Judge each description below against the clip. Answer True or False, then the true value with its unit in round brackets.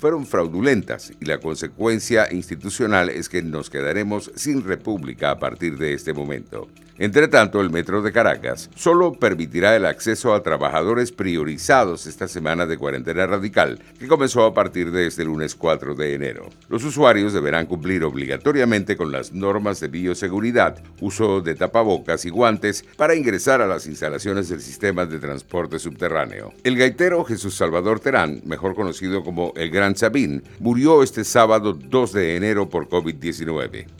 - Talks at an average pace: True (155 wpm)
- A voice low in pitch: True (95 Hz)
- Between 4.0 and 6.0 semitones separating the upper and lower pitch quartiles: True (4.9 semitones)